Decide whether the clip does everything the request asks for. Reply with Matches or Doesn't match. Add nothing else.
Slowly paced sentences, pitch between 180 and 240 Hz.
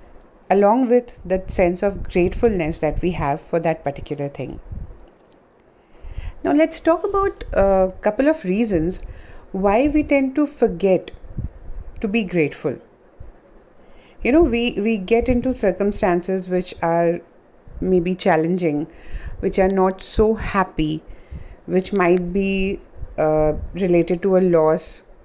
Matches